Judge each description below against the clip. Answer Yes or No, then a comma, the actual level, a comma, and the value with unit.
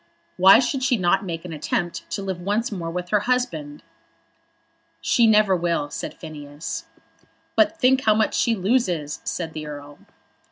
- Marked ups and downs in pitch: Yes, wide, 5.9 semitones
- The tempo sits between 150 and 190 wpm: Yes, average, 160 wpm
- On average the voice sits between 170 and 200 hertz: Yes, medium, 185 Hz